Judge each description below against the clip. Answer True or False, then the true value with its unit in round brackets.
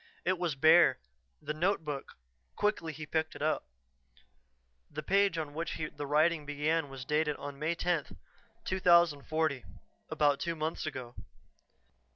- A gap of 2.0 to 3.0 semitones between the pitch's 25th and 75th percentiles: True (2.5 semitones)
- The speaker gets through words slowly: True (130 wpm)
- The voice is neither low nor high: True (155 Hz)